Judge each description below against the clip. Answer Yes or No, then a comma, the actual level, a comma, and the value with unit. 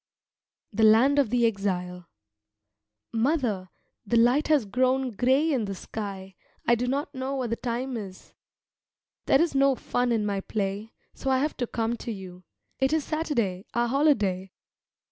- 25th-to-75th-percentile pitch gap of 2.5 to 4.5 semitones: No, average, 5.0 semitones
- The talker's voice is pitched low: No, high, 235 Hz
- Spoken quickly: No, average, 160 wpm